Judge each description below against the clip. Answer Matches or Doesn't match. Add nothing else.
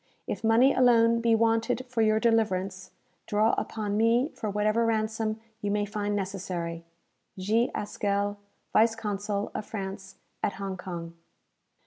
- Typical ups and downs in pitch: Doesn't match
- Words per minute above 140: Doesn't match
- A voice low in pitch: Doesn't match